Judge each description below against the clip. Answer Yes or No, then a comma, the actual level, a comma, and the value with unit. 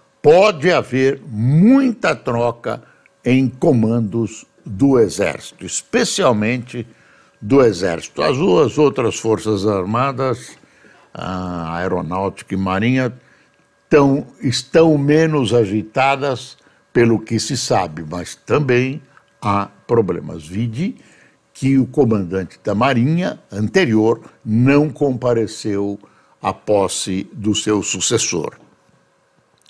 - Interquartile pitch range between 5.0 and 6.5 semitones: No, average, 4.4 semitones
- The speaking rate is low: Yes, slow, 95 wpm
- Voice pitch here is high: No, low, 120 Hz